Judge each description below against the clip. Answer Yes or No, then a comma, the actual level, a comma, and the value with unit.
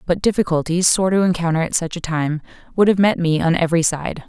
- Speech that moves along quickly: Yes, fast, 225 wpm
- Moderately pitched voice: Yes, medium, 170 Hz